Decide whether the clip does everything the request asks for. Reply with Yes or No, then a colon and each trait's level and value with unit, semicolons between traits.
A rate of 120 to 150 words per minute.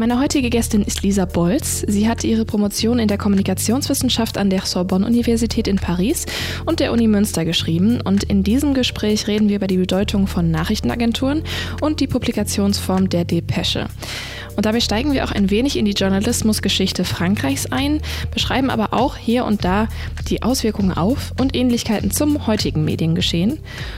No: average, 165 wpm